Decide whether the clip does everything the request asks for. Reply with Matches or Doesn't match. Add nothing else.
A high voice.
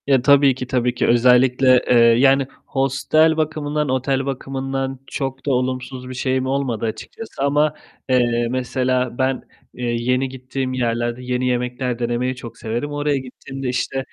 Doesn't match